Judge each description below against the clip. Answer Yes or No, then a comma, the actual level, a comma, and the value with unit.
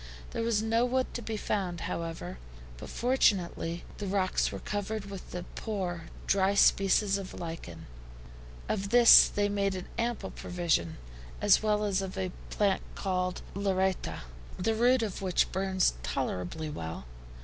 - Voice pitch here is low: No, high, 195 Hz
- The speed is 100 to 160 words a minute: Yes, average, 150 wpm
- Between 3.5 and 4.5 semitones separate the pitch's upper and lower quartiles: No, average, 2.8 semitones